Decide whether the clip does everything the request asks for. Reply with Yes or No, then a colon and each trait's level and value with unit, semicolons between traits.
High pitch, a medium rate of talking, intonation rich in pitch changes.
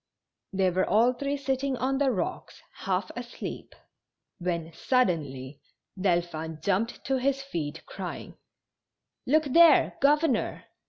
No: high, 230 Hz; slow, 120 wpm; wide, 7.7 semitones